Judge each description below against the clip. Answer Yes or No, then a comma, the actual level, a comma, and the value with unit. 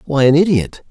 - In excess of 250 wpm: No, average, 200 wpm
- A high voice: No, medium, 145 Hz